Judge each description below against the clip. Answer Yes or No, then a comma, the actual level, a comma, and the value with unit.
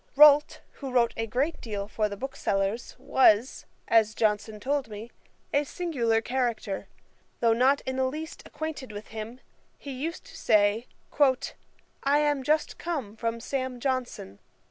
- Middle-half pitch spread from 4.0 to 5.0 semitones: Yes, average, 4.3 semitones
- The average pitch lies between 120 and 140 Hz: No, very high, 250 Hz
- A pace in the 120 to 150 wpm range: Yes, average, 145 wpm